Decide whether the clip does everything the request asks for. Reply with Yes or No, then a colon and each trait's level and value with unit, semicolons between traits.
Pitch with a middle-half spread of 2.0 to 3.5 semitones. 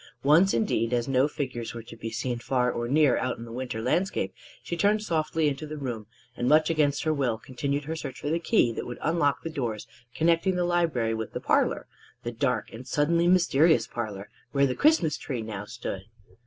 No: average, 5.3 semitones